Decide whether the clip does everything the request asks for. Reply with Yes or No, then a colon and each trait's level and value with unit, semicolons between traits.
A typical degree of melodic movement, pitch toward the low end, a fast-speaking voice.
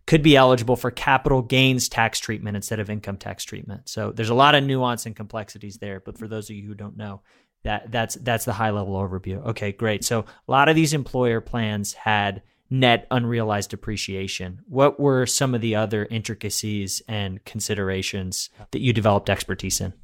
No: average, 3.2 semitones; low, 110 Hz; average, 190 wpm